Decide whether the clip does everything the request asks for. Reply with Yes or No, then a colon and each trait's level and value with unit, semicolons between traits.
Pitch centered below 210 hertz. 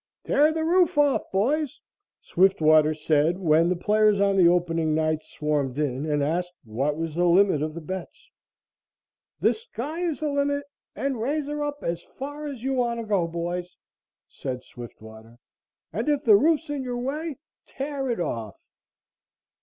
Yes: high, 190 Hz